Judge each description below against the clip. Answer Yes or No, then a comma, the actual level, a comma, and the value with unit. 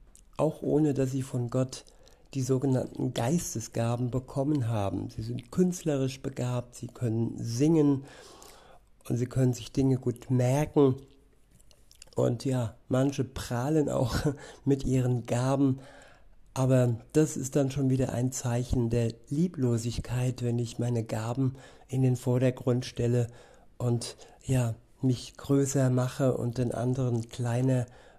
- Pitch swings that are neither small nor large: No, narrow, 2.0 semitones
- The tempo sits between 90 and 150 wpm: Yes, average, 130 wpm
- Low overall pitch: Yes, low, 125 Hz